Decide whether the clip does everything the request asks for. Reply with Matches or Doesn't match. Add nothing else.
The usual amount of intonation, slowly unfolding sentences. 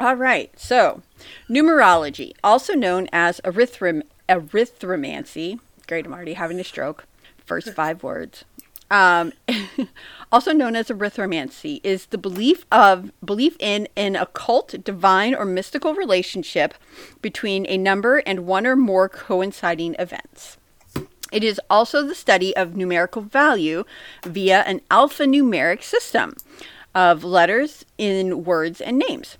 Doesn't match